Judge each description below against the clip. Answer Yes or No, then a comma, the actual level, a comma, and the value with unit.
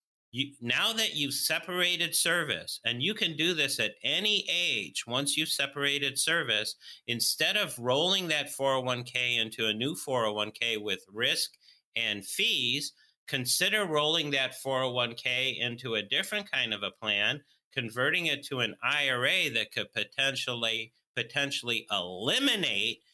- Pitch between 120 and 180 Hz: Yes, low, 135 Hz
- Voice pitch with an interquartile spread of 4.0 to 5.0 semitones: Yes, average, 4.6 semitones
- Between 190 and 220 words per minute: No, slow, 135 wpm